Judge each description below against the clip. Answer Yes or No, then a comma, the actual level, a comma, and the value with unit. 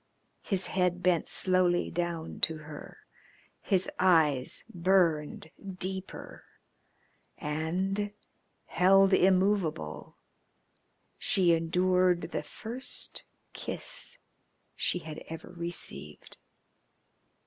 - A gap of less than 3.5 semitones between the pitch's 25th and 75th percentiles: Yes, average, 2.7 semitones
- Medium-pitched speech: Yes, medium, 180 Hz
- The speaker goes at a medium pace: No, slow, 80 wpm